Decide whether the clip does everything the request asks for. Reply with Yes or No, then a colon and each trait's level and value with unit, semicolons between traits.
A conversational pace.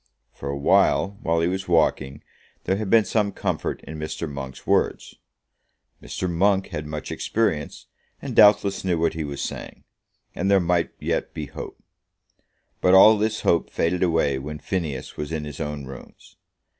Yes: average, 170 wpm